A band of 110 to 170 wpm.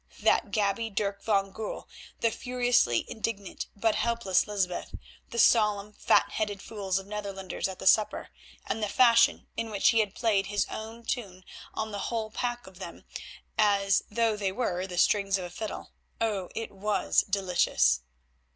Yes: average, 160 wpm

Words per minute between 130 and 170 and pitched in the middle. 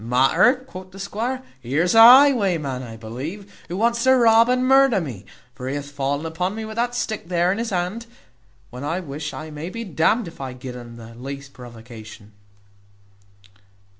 No: average, 190 wpm; medium, 170 Hz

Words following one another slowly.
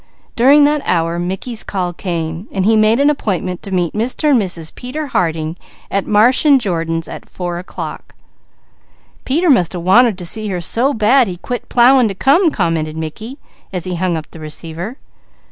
No: average, 180 wpm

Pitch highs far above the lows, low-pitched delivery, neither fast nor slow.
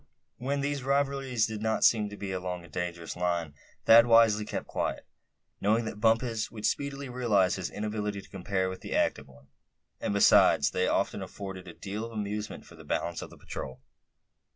No: average, 3.8 semitones; low, 105 Hz; average, 185 wpm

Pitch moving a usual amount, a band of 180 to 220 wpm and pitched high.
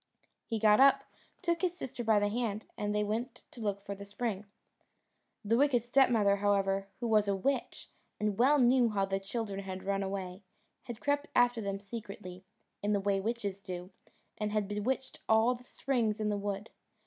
Yes: average, 3.3 semitones; average, 185 wpm; high, 210 Hz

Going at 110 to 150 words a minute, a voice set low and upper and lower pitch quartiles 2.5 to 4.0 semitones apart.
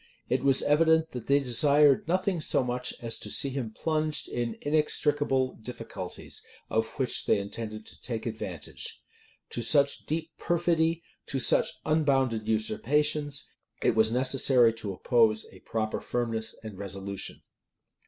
No: average, 140 wpm; low, 130 Hz; average, 5.1 semitones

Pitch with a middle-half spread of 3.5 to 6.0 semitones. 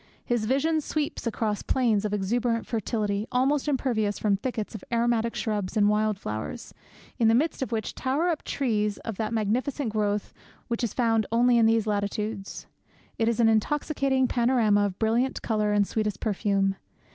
No: average, 2.9 semitones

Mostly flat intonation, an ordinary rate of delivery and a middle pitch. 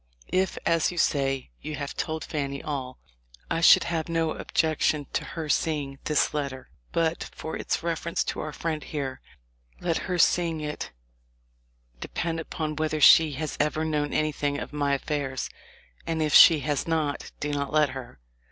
Yes: narrow, 2.2 semitones; average, 165 wpm; medium, 155 Hz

